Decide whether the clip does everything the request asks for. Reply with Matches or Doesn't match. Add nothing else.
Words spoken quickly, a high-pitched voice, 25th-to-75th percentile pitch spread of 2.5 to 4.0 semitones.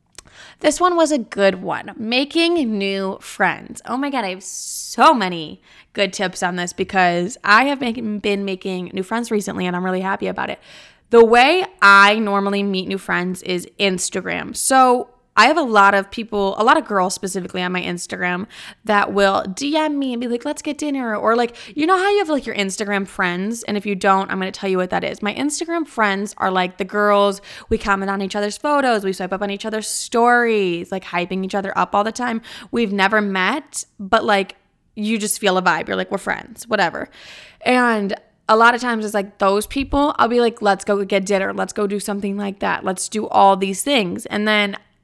Matches